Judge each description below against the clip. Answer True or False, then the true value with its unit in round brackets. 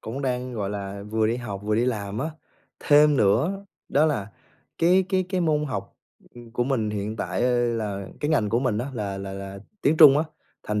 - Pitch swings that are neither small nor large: False (5.9 semitones)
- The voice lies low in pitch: True (120 Hz)